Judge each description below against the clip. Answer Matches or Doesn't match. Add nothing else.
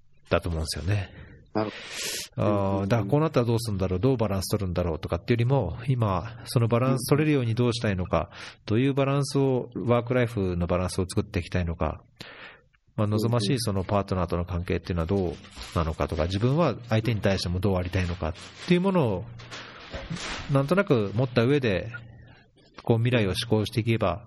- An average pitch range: Matches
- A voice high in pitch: Doesn't match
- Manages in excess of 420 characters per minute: Matches